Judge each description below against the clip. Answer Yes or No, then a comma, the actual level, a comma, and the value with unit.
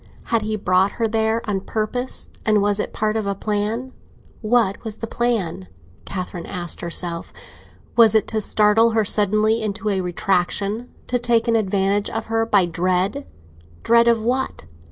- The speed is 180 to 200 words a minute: No, average, 160 wpm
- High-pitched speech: Yes, high, 215 Hz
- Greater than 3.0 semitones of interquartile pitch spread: No, narrow, 2.6 semitones